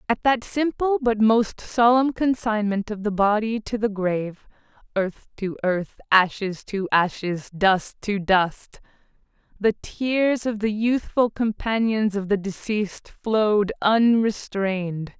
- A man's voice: No, female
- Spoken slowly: Yes, slow, 125 wpm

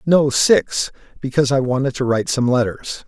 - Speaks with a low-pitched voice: Yes, low, 130 Hz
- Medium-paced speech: Yes, average, 155 wpm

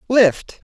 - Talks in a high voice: Yes, high, 215 Hz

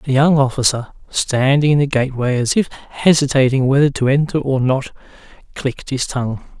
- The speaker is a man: Yes, male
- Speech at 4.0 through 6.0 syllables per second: Yes, 5.5 syllables/s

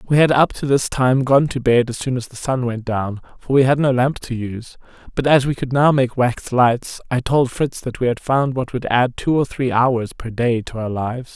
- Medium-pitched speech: No, low, 125 Hz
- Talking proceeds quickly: Yes, fast, 265 wpm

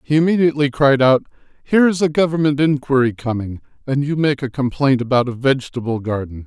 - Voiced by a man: Yes, male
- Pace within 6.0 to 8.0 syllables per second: Yes, 6.1 syllables/s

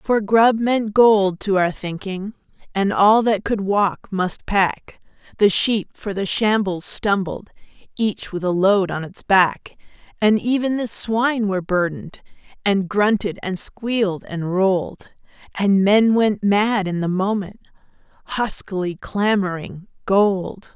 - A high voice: Yes, high, 200 Hz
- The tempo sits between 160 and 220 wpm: No, average, 140 wpm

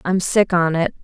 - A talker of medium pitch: Yes, medium, 175 Hz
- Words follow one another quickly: Yes, fast, 230 wpm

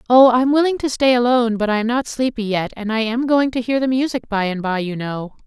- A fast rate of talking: Yes, fast, 275 wpm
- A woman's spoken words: Yes, female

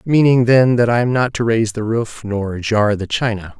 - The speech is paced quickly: Yes, fast, 235 wpm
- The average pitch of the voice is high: No, low, 115 Hz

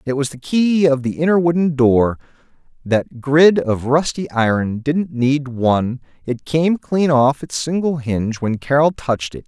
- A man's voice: Yes, male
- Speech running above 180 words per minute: No, average, 165 wpm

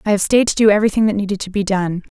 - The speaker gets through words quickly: Yes, fast, 300 wpm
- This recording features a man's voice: No, female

